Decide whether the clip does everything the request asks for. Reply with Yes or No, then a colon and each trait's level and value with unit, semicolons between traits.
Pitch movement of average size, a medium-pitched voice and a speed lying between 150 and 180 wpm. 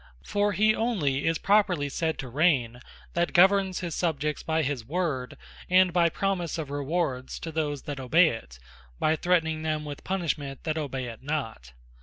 Yes: average, 4.3 semitones; medium, 155 Hz; average, 175 wpm